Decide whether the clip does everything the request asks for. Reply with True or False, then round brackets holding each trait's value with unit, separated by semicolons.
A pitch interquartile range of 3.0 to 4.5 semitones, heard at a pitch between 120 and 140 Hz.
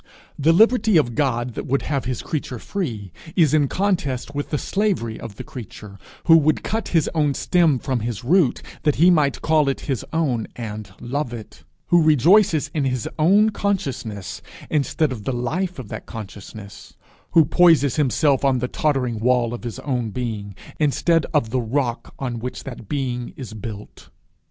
False (4.9 semitones; 135 Hz)